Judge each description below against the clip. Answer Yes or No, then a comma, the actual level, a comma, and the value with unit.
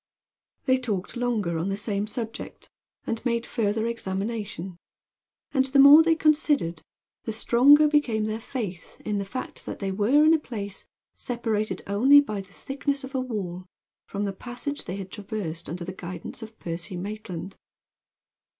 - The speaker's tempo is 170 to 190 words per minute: No, average, 160 wpm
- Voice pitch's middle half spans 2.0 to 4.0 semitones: No, average, 4.9 semitones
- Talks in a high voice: Yes, high, 215 Hz